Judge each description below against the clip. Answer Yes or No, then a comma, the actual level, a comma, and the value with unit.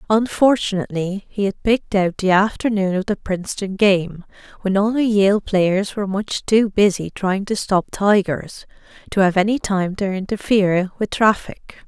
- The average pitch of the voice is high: Yes, high, 200 Hz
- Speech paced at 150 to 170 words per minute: Yes, average, 160 wpm